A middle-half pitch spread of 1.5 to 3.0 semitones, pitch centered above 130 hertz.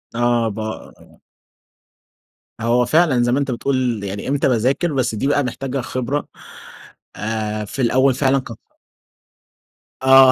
No: narrow, 2.6 semitones; low, 125 Hz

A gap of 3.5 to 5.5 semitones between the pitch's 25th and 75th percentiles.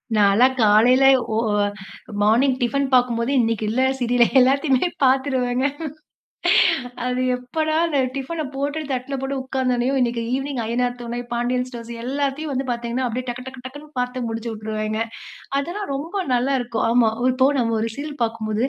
No: narrow, 2.5 semitones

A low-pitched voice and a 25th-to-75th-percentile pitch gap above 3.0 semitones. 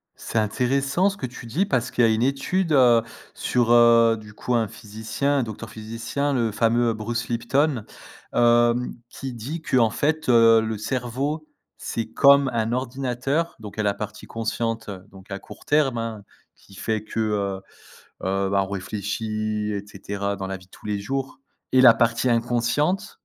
Yes: low, 115 Hz; average, 3.4 semitones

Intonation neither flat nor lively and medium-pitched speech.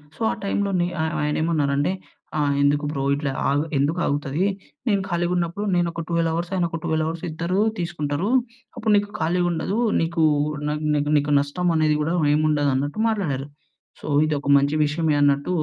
Yes: average, 3.1 semitones; medium, 160 Hz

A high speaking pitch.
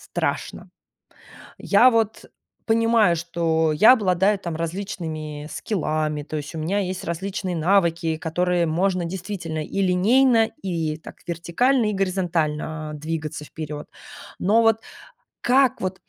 No: medium, 175 Hz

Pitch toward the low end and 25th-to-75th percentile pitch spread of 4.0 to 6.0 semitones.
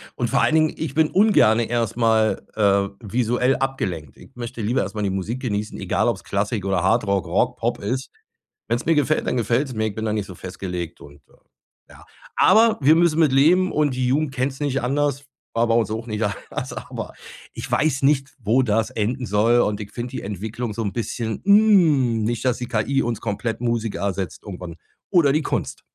Yes: low, 120 Hz; average, 4.5 semitones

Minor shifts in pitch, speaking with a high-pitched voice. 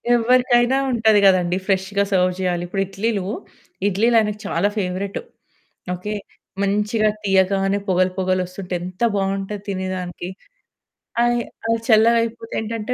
No: average, 3.1 semitones; high, 195 Hz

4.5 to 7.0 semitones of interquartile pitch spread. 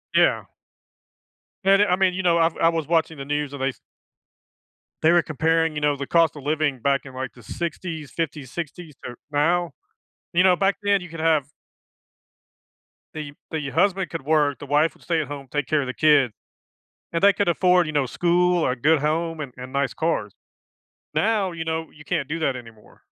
No: average, 3.2 semitones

